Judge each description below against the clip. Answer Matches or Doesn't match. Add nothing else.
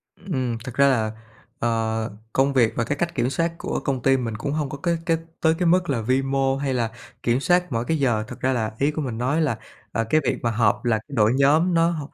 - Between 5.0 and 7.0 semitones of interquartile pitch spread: Doesn't match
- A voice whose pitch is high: Doesn't match